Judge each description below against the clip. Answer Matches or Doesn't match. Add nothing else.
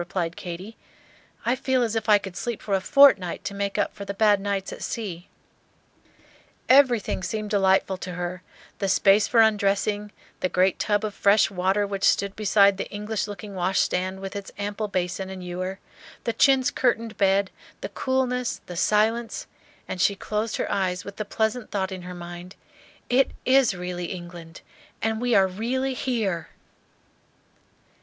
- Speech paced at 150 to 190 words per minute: Matches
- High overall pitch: Matches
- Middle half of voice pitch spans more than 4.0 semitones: Doesn't match